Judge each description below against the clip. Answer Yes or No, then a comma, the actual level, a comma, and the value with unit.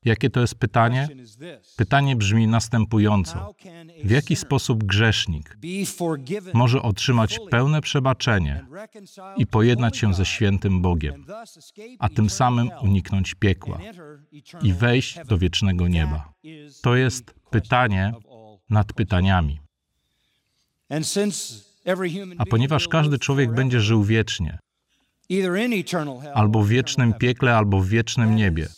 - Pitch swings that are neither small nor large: No, wide, 5.7 semitones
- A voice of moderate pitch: No, low, 120 Hz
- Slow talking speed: Yes, slow, 105 wpm